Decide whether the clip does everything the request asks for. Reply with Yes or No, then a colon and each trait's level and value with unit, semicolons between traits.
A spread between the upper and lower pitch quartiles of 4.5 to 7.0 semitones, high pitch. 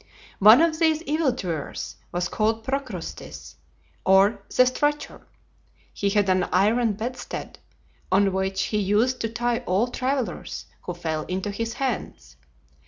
Yes: average, 4.9 semitones; high, 215 Hz